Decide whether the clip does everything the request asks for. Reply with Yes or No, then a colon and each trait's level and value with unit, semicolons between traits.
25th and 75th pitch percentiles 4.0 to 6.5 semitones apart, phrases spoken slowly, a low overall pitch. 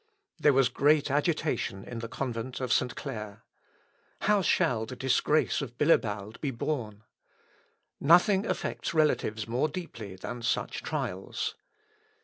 Yes: average, 5.1 semitones; slow, 130 wpm; low, 130 Hz